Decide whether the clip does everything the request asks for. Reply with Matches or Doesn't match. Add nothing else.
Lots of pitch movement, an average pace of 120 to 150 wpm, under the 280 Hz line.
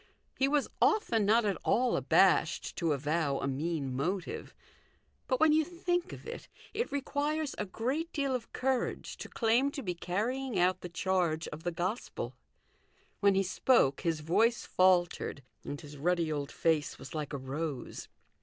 Doesn't match